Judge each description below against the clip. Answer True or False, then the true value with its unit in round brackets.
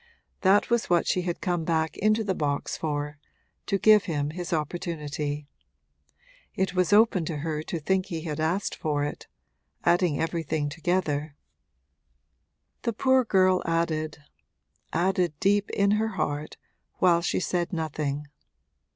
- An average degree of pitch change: True (3.7 semitones)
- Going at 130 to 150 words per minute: True (140 wpm)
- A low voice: False (170 Hz)